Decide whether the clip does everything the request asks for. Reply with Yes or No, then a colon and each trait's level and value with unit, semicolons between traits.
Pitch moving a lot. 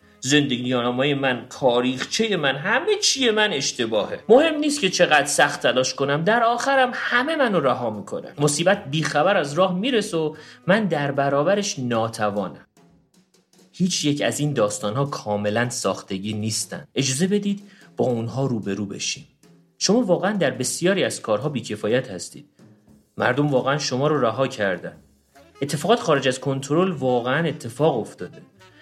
Yes: wide, 7.4 semitones